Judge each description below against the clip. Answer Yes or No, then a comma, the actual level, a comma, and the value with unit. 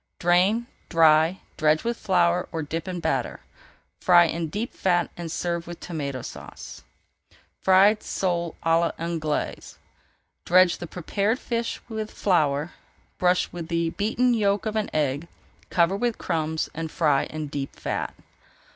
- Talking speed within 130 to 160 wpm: Yes, average, 140 wpm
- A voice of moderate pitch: Yes, medium, 170 Hz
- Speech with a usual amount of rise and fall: Yes, average, 3.4 semitones